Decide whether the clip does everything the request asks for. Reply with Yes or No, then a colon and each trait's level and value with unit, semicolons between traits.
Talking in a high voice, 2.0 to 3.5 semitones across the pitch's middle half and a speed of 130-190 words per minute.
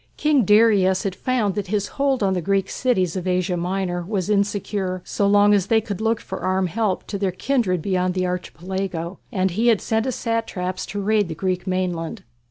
No: high, 195 Hz; narrow, 2.6 semitones; average, 200 wpm